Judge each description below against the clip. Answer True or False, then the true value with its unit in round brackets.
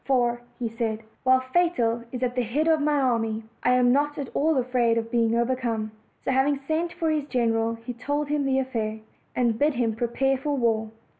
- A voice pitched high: True (250 Hz)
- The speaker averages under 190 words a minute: False (205 wpm)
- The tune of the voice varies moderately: True (3.6 semitones)